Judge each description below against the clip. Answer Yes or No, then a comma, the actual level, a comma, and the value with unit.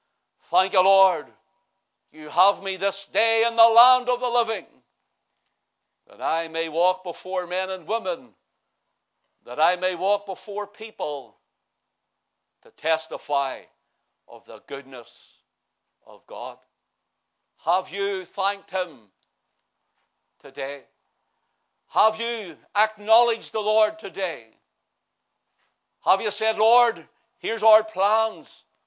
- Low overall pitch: No, high, 200 Hz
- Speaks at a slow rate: Yes, slow, 110 wpm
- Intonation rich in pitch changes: No, average, 3.5 semitones